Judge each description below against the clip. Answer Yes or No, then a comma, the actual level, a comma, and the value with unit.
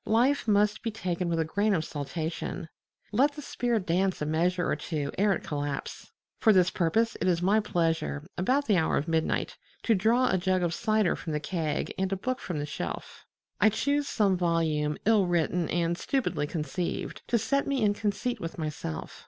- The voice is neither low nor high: Yes, medium, 180 Hz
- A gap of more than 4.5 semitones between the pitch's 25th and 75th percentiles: Yes, average, 5.0 semitones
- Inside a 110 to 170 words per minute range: No, average, 195 wpm